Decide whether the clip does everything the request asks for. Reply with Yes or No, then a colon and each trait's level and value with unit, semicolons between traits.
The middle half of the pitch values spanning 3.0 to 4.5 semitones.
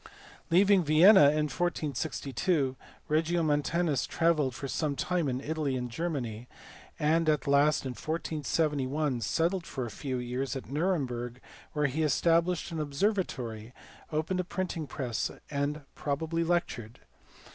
Yes: average, 4.0 semitones